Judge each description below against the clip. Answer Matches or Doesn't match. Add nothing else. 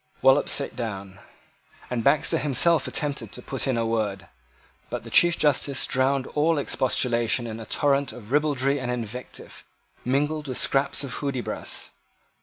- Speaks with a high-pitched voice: Doesn't match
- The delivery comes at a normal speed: Matches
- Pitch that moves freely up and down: Doesn't match